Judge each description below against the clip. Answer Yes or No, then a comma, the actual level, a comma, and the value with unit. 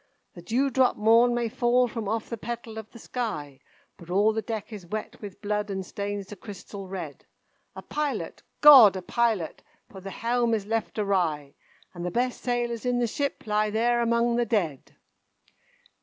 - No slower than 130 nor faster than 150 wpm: No, average, 180 wpm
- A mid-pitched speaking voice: No, high, 220 Hz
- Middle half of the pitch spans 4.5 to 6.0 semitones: No, average, 3.4 semitones